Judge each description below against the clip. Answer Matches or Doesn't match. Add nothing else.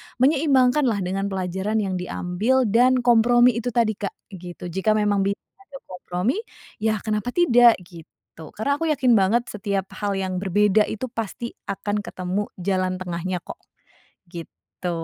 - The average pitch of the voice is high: Matches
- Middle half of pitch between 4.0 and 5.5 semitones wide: Matches